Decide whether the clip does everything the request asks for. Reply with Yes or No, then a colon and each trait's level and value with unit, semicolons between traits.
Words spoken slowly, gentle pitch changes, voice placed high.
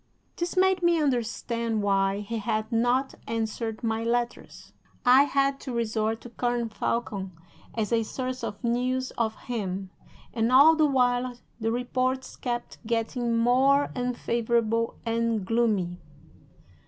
Yes: slow, 130 wpm; narrow, 2.3 semitones; high, 235 Hz